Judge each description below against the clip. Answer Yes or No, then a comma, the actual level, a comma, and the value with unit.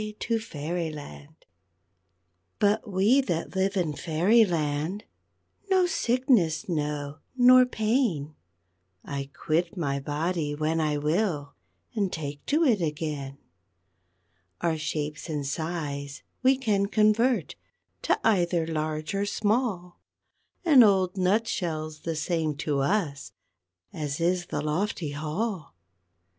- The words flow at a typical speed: No, slow, 115 wpm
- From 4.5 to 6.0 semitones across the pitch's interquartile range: Yes, wide, 5.6 semitones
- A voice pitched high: No, medium, 170 Hz